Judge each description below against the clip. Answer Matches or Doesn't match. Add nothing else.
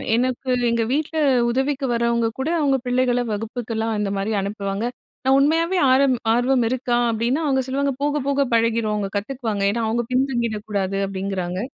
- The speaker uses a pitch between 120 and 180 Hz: Doesn't match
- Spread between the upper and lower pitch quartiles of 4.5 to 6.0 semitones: Doesn't match